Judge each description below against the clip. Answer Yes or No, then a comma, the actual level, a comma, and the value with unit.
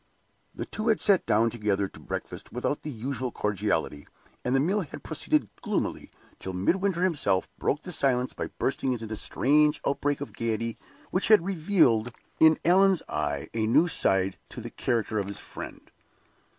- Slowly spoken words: No, average, 170 wpm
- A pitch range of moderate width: No, wide, 7.3 semitones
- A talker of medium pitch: No, low, 130 Hz